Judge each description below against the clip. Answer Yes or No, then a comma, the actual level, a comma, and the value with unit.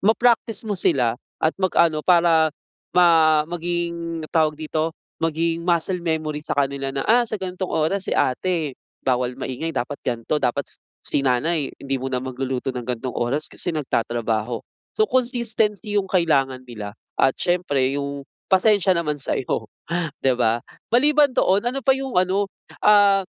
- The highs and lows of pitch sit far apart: Yes, wide, 6.1 semitones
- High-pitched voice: No, medium, 160 Hz